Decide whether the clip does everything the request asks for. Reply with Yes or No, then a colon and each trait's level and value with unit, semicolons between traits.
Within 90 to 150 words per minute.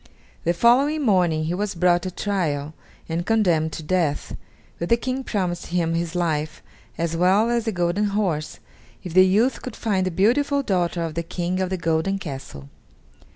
No: average, 180 wpm